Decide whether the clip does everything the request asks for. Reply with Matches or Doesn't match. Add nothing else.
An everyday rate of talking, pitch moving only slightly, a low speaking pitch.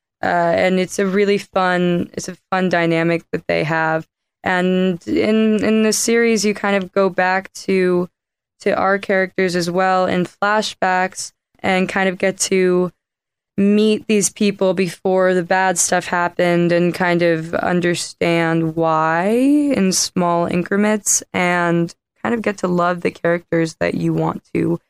Doesn't match